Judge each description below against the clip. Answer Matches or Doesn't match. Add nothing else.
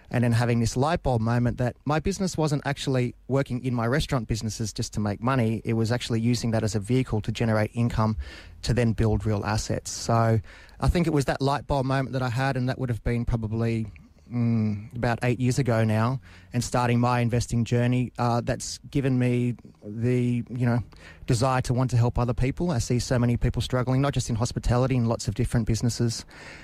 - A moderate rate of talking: Doesn't match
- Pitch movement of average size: Doesn't match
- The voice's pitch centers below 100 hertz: Doesn't match